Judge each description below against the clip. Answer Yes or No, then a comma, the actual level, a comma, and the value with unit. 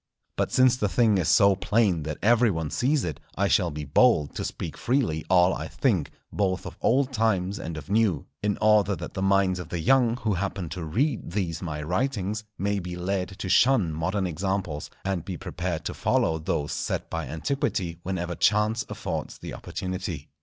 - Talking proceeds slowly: No, average, 190 wpm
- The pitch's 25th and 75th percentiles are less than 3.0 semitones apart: No, average, 4.3 semitones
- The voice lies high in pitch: No, very low, 95 Hz